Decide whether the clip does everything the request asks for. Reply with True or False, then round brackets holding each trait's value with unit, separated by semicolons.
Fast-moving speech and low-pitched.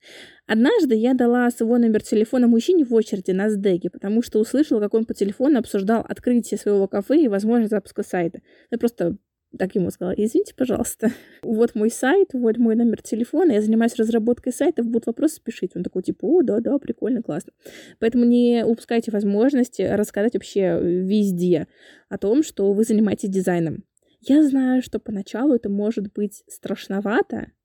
False (165 wpm; 225 Hz)